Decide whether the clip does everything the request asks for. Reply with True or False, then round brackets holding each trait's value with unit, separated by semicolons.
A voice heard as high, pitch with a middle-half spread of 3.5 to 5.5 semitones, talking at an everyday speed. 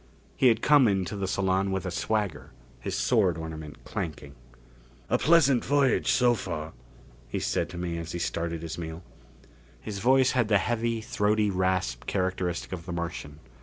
False (95 Hz; 4.8 semitones; 165 wpm)